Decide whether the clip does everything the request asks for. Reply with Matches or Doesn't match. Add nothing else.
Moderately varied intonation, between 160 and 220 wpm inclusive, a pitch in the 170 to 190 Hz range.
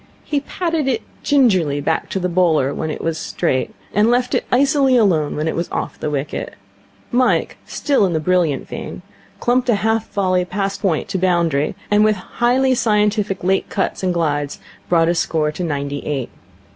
Doesn't match